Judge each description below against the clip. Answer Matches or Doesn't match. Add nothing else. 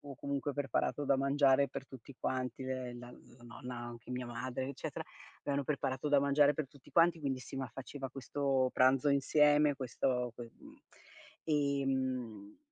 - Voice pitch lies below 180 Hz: Matches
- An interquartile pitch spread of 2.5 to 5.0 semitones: Doesn't match